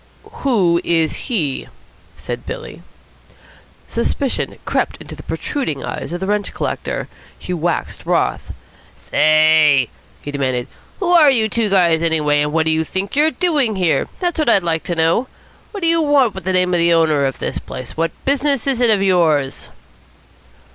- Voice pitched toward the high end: No, medium, 180 Hz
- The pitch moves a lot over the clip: Yes, wide, 8.4 semitones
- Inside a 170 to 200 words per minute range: Yes, average, 175 wpm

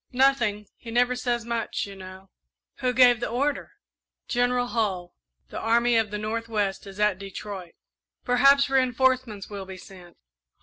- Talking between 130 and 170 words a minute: Yes, average, 155 wpm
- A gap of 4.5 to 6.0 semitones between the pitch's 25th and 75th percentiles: No, average, 3.8 semitones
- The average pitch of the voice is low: No, high, 230 Hz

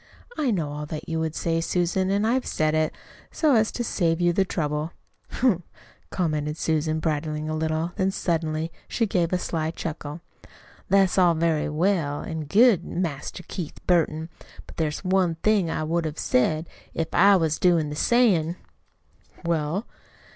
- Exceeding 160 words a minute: Yes, average, 170 wpm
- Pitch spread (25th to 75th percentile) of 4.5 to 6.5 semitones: No, average, 3.1 semitones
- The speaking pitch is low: No, medium, 165 Hz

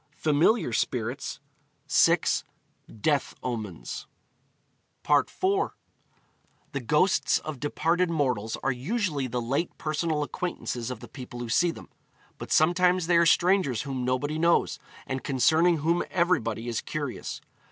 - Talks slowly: Yes, slow, 125 wpm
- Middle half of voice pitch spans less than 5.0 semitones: No, average, 5.3 semitones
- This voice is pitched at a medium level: Yes, medium, 145 Hz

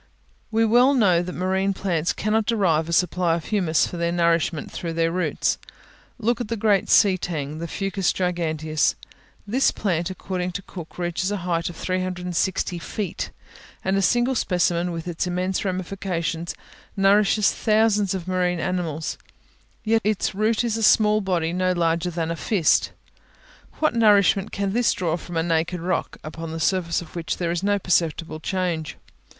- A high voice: No, medium, 180 Hz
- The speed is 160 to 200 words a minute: Yes, average, 165 wpm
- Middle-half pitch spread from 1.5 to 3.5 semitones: Yes, average, 3.1 semitones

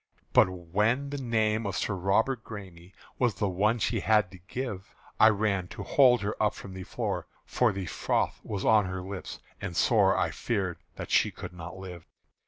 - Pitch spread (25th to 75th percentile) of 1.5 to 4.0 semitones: Yes, average, 3.1 semitones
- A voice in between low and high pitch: No, low, 100 Hz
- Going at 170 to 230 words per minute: Yes, average, 190 wpm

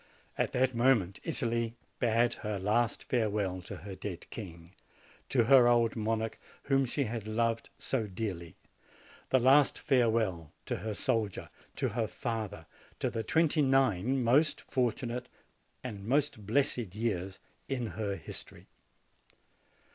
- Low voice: Yes, low, 115 Hz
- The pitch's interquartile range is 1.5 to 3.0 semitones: No, average, 3.6 semitones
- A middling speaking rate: No, slow, 130 wpm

